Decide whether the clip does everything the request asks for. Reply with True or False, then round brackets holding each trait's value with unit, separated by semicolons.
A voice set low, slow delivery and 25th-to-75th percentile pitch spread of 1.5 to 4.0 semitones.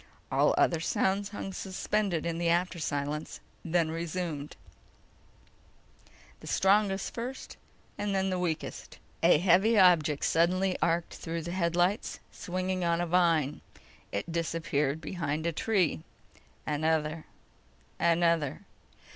False (170 Hz; 115 wpm; 2.7 semitones)